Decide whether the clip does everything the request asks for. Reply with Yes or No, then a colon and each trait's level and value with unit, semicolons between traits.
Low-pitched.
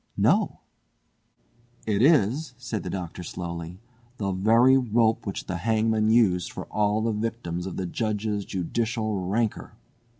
Yes: low, 110 Hz